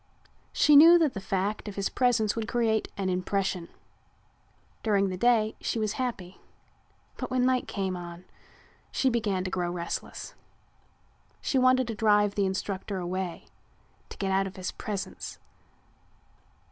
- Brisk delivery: No, average, 145 wpm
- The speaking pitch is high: Yes, high, 200 Hz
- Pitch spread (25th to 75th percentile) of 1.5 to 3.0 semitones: No, average, 3.8 semitones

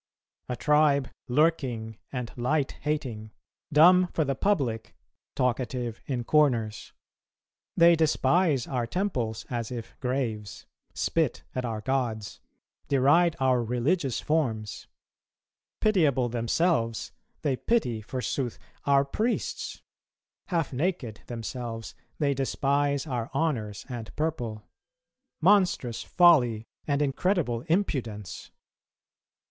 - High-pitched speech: No, low, 130 Hz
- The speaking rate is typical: No, slow, 100 wpm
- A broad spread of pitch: No, average, 4.9 semitones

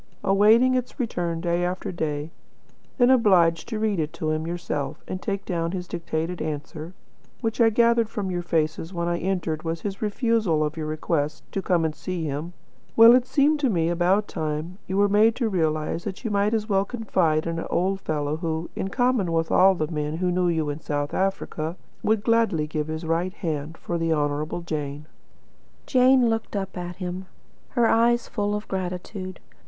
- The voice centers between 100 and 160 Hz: No, medium, 175 Hz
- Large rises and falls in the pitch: No, average, 4.6 semitones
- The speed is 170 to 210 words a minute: Yes, average, 190 wpm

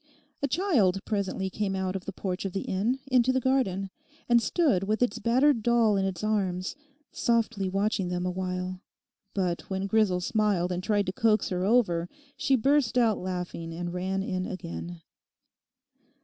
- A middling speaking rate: Yes, average, 165 wpm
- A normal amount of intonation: Yes, average, 4.0 semitones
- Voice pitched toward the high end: Yes, high, 195 Hz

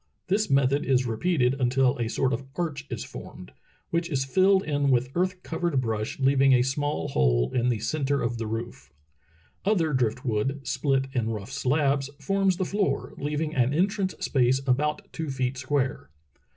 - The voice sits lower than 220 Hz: Yes, low, 135 Hz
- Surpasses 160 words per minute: Yes, average, 170 wpm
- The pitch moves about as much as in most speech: Yes, average, 3.8 semitones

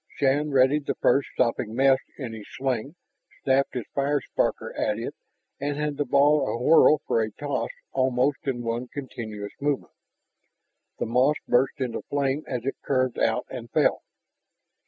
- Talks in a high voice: No, low, 130 Hz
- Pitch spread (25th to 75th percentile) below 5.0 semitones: Yes, average, 2.8 semitones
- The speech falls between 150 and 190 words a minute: Yes, average, 155 wpm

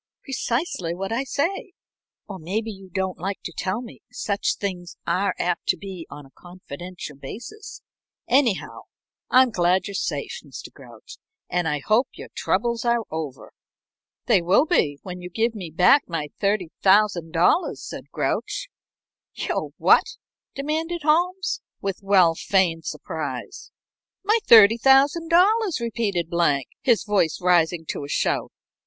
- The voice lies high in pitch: Yes, high, 195 Hz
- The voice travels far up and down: Yes, wide, 6.4 semitones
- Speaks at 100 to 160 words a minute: Yes, slow, 135 wpm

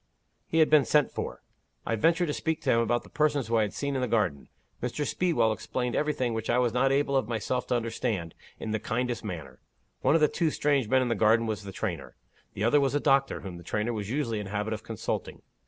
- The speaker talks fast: Yes, fast, 250 wpm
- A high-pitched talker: No, low, 120 Hz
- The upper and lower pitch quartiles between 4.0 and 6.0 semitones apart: Yes, average, 4.5 semitones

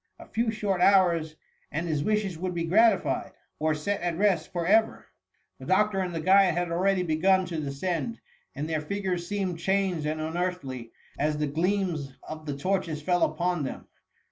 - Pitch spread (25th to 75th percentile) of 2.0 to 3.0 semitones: No, average, 3.6 semitones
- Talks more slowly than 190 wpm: Yes, average, 175 wpm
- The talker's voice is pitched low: No, medium, 175 Hz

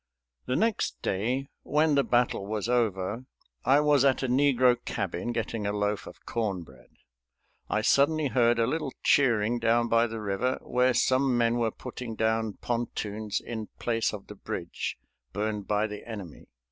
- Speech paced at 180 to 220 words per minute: No, average, 165 wpm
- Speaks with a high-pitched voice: No, low, 115 Hz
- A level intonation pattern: No, average, 3.3 semitones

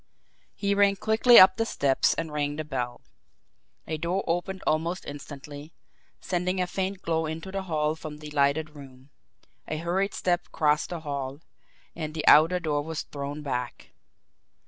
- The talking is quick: No, average, 160 wpm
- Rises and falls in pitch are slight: No, average, 3.7 semitones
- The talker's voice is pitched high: No, medium, 155 Hz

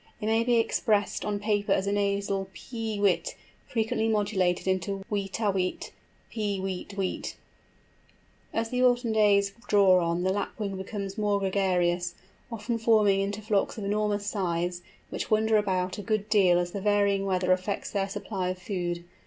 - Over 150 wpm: Yes, average, 165 wpm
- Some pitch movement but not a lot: No, narrow, 2.1 semitones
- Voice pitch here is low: No, high, 200 Hz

